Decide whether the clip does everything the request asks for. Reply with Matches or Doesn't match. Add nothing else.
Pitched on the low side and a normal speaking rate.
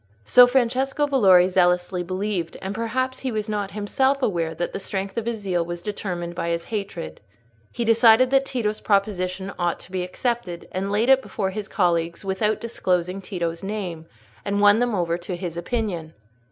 Doesn't match